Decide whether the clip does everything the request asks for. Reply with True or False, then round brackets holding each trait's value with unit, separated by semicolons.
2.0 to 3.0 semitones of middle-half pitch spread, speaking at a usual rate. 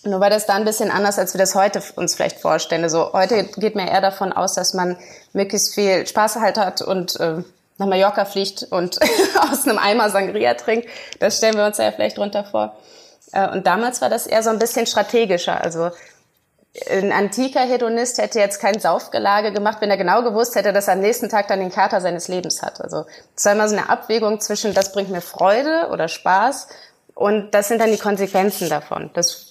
False (2.5 semitones; 210 wpm)